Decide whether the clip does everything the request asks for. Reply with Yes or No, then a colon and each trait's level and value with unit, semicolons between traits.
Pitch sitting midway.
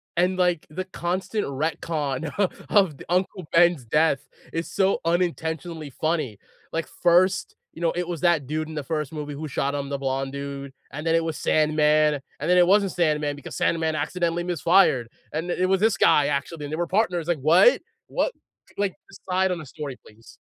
Yes: medium, 160 Hz